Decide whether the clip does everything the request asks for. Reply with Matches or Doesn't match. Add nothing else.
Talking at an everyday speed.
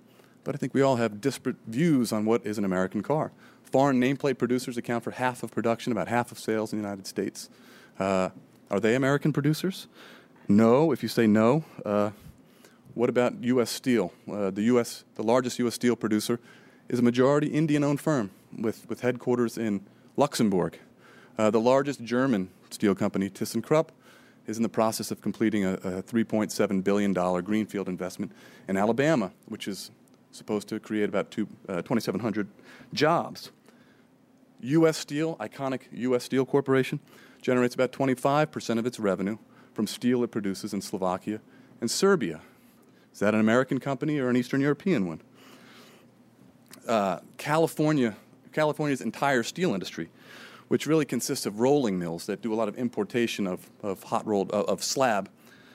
Matches